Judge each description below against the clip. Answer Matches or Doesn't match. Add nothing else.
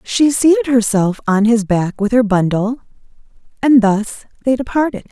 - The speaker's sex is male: Doesn't match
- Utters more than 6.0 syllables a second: Doesn't match